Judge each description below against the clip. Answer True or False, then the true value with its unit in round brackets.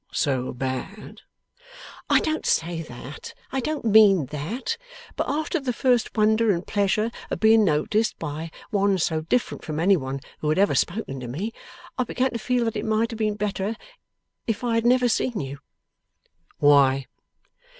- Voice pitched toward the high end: True (205 Hz)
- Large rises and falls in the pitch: True (6.9 semitones)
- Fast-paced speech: False (170 wpm)